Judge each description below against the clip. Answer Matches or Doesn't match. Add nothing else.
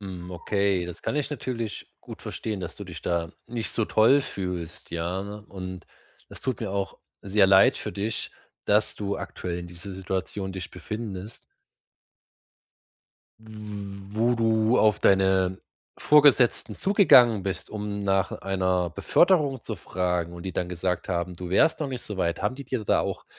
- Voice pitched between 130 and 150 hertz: Doesn't match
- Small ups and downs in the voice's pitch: Doesn't match